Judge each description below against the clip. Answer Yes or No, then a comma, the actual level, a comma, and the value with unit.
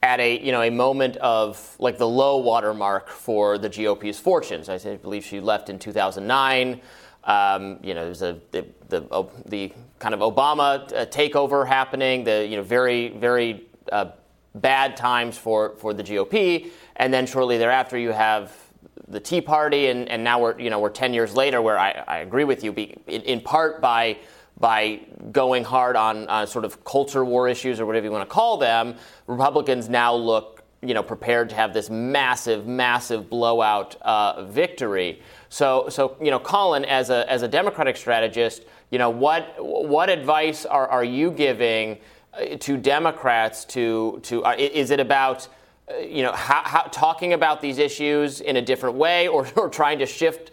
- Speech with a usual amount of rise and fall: Yes, average, 3.5 semitones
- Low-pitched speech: Yes, low, 120 Hz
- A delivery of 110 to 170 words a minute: No, average, 185 wpm